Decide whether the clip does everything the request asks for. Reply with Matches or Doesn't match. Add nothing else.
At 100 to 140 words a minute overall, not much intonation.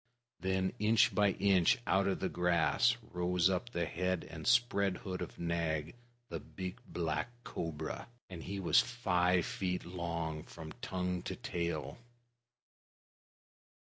Matches